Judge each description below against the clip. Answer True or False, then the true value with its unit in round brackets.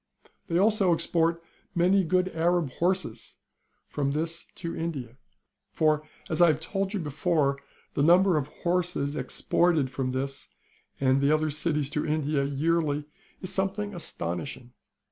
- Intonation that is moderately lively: True (3.8 semitones)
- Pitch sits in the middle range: True (160 Hz)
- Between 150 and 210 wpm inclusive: False (140 wpm)